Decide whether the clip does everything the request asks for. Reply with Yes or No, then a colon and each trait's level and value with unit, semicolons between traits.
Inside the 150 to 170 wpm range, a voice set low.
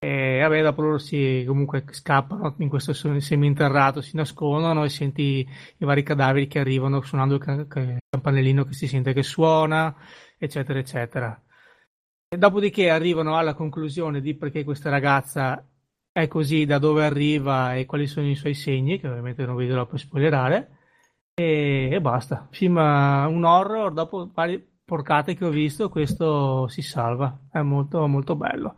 No: average, 165 wpm; medium, 145 Hz